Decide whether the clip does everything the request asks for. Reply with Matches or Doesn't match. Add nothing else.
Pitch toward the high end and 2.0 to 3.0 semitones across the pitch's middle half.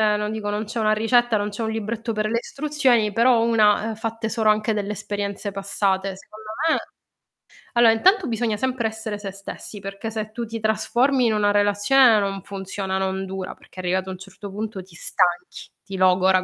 Matches